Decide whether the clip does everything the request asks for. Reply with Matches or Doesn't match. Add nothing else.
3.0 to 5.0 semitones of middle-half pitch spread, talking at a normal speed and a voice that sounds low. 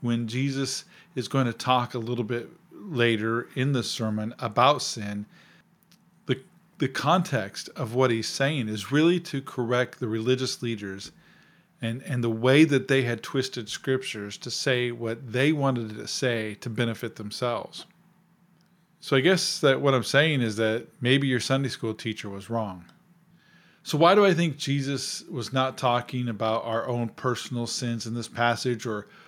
Matches